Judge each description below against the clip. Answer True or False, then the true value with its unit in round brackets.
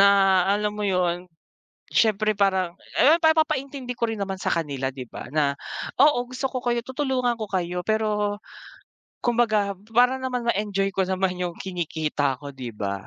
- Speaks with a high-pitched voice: True (200 Hz)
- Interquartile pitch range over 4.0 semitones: True (5.5 semitones)